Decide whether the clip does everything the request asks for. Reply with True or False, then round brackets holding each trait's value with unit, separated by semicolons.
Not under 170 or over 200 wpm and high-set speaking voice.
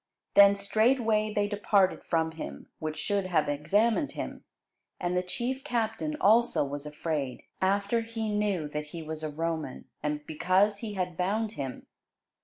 False (155 wpm; 195 Hz)